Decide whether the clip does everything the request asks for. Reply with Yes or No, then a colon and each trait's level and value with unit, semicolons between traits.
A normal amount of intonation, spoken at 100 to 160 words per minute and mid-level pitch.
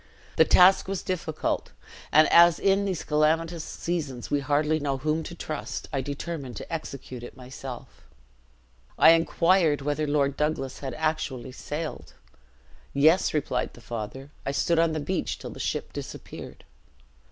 Yes: average, 3.3 semitones; average, 150 wpm; medium, 150 Hz